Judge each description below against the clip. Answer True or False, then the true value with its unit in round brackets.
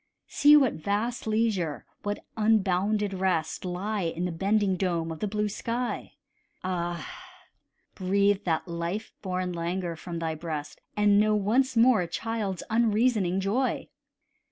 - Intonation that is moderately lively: True (3.7 semitones)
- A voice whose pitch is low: False (195 Hz)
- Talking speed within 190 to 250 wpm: False (135 wpm)